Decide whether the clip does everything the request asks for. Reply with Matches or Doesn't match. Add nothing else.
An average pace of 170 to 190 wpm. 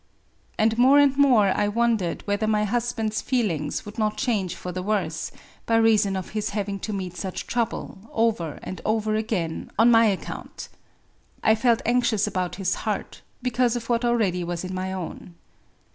Matches